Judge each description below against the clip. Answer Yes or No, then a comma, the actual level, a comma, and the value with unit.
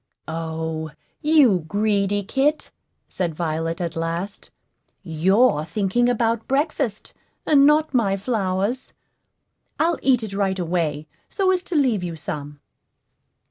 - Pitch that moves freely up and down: Yes, wide, 7.3 semitones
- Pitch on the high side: Yes, high, 200 Hz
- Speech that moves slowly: Yes, slow, 120 wpm